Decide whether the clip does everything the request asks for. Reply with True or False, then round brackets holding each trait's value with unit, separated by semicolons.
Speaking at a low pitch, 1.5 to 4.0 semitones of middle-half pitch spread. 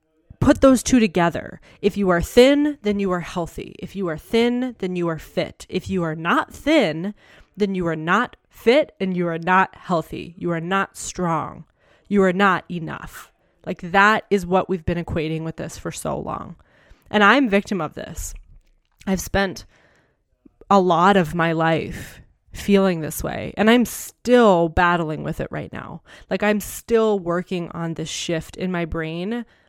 False (185 Hz; 3.5 semitones)